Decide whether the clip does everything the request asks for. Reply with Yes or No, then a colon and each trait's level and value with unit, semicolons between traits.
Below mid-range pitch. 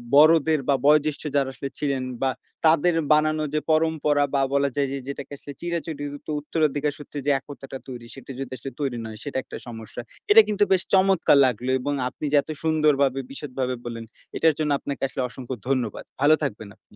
No: medium, 145 Hz